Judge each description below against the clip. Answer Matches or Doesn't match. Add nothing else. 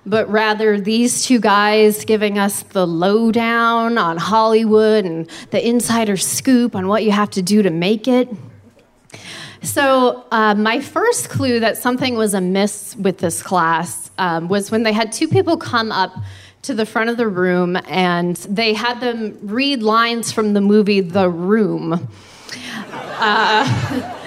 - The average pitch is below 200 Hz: Doesn't match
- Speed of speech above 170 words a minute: Doesn't match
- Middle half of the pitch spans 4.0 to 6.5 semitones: Doesn't match